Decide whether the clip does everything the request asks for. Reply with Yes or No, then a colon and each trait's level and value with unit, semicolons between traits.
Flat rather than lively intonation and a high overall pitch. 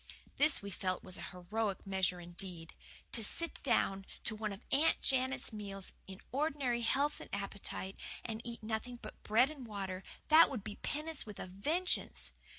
No: wide, 5.6 semitones; high, 215 Hz